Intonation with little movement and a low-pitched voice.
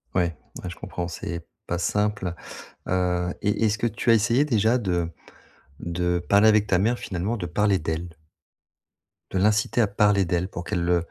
No: average, 3.2 semitones; very low, 95 Hz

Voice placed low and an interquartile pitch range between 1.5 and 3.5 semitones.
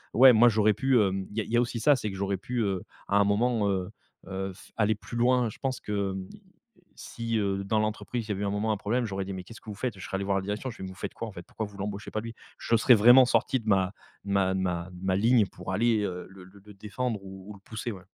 Yes: low, 105 Hz; average, 2.9 semitones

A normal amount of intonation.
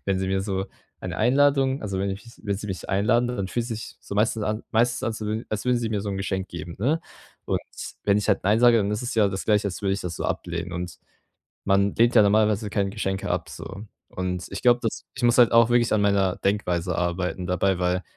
Yes: average, 3.1 semitones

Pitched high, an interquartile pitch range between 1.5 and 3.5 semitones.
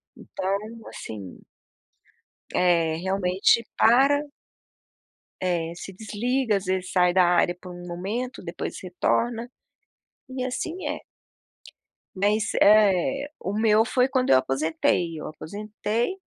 No: high, 200 Hz; average, 4.8 semitones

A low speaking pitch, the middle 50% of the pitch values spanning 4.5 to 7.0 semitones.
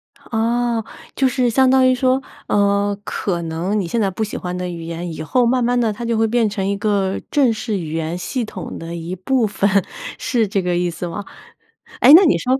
No: high, 210 Hz; average, 5.3 semitones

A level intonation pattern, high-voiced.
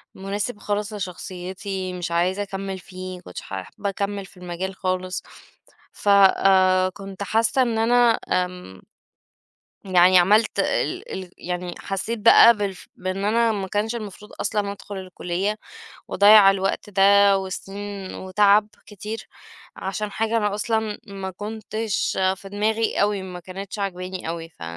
Yes: narrow, 2.1 semitones; high, 195 Hz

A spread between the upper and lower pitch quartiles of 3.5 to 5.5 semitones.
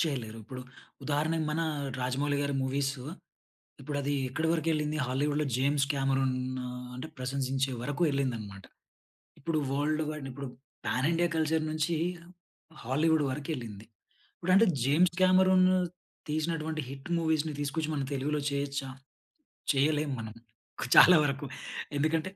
No: average, 2.8 semitones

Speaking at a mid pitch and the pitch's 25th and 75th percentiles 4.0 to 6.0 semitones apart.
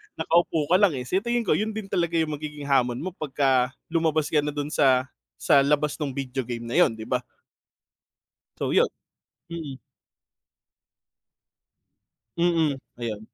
Yes: medium, 150 Hz; average, 4.3 semitones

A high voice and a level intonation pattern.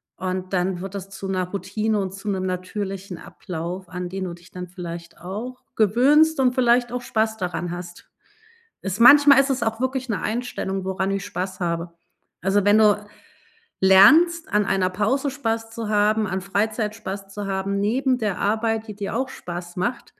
No: high, 200 Hz; average, 3.3 semitones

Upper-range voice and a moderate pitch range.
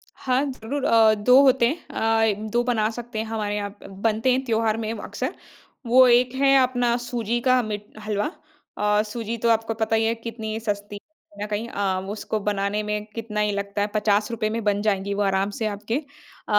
No: high, 220 Hz; narrow, 2.3 semitones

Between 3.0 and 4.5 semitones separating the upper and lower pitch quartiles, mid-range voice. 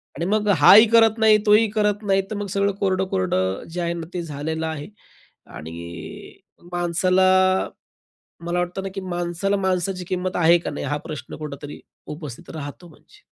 Yes: average, 4.1 semitones; medium, 175 Hz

